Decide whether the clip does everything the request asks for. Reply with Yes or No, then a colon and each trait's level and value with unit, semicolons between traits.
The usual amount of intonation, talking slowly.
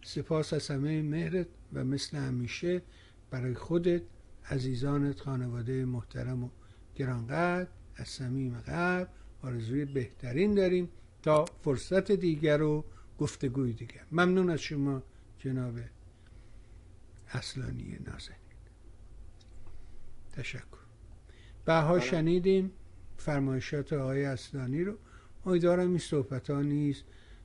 No: wide, 6.4 semitones; slow, 95 wpm